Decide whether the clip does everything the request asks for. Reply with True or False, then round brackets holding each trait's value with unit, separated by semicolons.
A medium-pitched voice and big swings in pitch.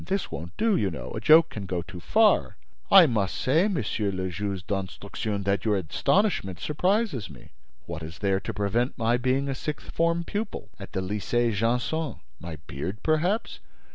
False (110 Hz; 8.9 semitones)